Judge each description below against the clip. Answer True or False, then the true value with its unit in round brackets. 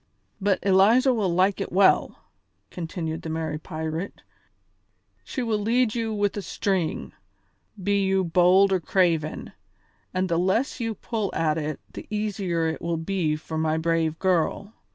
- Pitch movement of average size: True (3.9 semitones)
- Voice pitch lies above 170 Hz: True (185 Hz)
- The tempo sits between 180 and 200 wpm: False (155 wpm)